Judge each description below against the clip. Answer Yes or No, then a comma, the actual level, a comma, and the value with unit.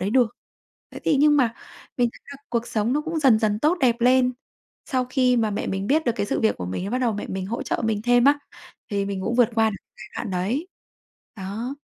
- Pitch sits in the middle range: No, high, 235 Hz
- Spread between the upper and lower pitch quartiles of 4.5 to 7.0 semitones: No, average, 3.9 semitones